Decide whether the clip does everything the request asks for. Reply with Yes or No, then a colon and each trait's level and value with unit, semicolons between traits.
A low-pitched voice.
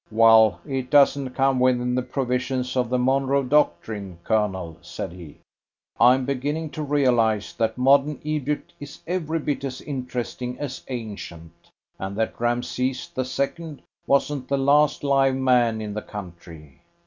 Yes: low, 125 Hz